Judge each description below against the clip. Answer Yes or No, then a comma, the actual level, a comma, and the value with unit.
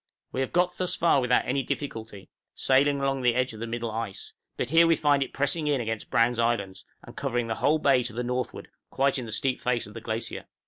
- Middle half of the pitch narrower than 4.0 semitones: Yes, average, 3.3 semitones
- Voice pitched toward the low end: Yes, low, 125 Hz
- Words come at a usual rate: No, fast, 240 wpm